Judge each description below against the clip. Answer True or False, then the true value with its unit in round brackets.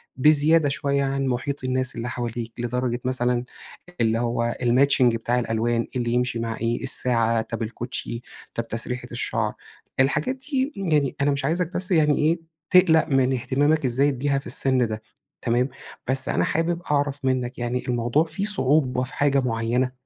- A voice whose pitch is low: True (130 Hz)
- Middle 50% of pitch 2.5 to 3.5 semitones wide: True (3.2 semitones)